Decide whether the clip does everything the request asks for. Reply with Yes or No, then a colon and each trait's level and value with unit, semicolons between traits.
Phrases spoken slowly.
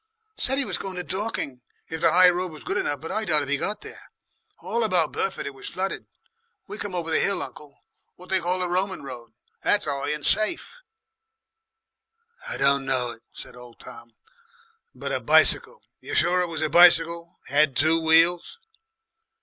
No: average, 185 wpm